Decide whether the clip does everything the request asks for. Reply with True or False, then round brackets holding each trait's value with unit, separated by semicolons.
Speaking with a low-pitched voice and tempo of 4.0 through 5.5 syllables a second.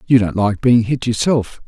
True (115 Hz; 4.6 syllables/s)